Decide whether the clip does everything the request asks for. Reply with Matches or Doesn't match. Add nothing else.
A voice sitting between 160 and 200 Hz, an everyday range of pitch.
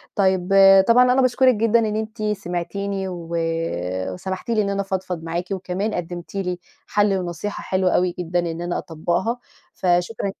Matches